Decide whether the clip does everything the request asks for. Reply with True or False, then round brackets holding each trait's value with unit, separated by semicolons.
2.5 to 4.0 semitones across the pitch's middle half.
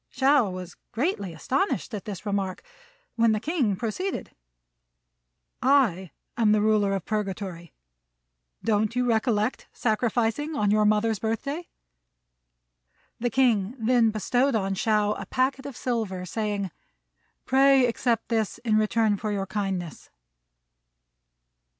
True (3.5 semitones)